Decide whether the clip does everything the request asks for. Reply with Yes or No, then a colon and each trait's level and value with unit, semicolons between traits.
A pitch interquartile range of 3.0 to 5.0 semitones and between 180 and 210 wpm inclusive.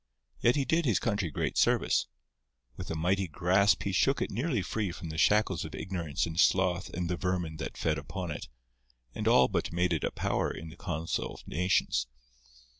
Yes: average, 3.3 semitones; average, 195 wpm